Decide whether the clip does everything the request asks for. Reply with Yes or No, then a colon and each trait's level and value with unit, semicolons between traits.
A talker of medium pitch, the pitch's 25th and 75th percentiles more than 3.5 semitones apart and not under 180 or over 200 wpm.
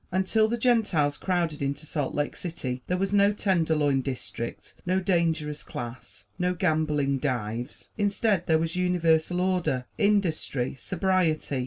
No: medium, 165 Hz; average, 4.5 semitones; slow, 135 wpm